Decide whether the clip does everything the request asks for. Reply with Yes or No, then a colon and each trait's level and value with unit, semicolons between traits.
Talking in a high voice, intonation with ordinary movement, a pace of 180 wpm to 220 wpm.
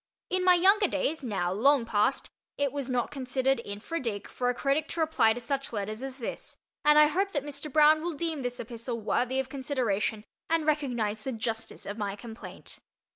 Yes: very high, 265 Hz; average, 4.9 semitones; average, 195 wpm